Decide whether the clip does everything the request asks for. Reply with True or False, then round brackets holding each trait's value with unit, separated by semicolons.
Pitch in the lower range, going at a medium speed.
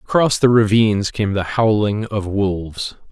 True (105 Hz; 155 wpm)